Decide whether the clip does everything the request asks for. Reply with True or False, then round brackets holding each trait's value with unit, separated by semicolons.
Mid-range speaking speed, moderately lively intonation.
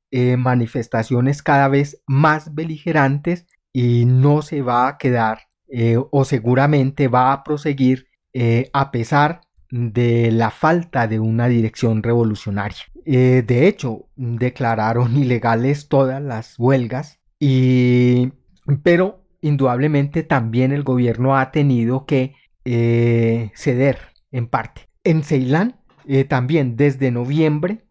False (120 wpm; 3.1 semitones)